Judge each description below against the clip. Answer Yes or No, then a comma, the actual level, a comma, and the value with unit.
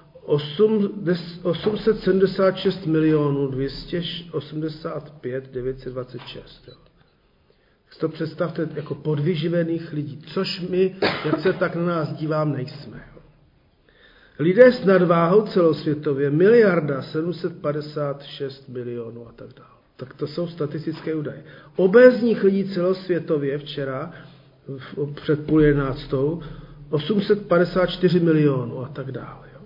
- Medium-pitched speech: Yes, medium, 155 Hz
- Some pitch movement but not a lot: Yes, average, 3.7 semitones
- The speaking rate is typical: No, slow, 95 wpm